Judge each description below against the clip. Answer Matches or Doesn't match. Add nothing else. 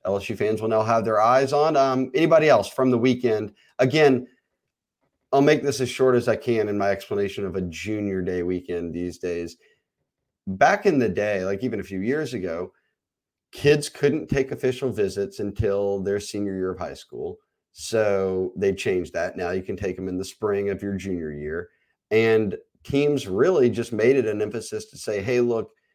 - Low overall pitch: Matches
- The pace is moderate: Matches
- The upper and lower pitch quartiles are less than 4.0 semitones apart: Doesn't match